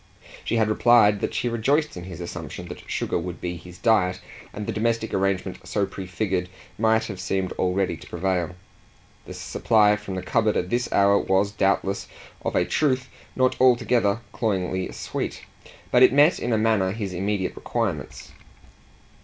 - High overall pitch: No, low, 100 Hz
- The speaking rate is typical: Yes, average, 165 wpm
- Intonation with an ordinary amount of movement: Yes, average, 3.5 semitones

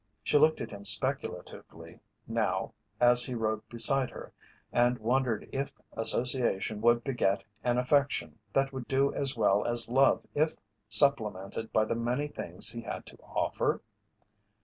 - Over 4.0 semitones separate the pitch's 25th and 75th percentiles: No, average, 3.6 semitones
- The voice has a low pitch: Yes, low, 120 Hz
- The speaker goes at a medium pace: Yes, average, 150 wpm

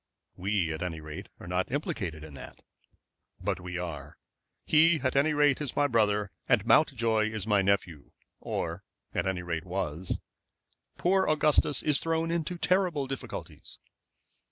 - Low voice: Yes, low, 110 Hz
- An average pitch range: No, wide, 8.7 semitones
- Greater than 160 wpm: No, average, 150 wpm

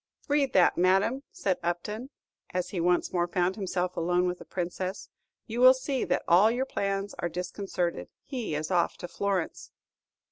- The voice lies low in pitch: No, medium, 185 Hz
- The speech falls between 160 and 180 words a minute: Yes, average, 170 wpm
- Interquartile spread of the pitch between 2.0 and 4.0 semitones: Yes, average, 3.5 semitones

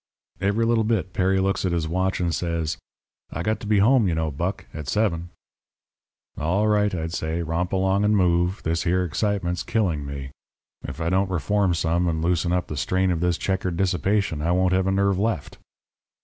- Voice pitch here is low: Yes, very low, 90 Hz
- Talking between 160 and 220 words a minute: Yes, average, 195 wpm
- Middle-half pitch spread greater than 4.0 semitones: No, average, 2.9 semitones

